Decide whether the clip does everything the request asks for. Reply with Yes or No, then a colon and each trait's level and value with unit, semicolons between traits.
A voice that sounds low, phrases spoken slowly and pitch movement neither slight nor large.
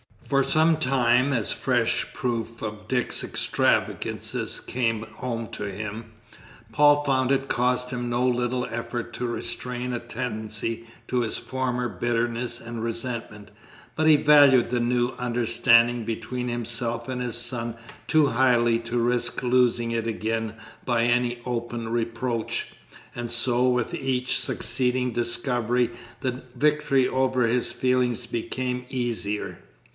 No: low, 120 Hz; slow, 130 wpm; narrow, 1.5 semitones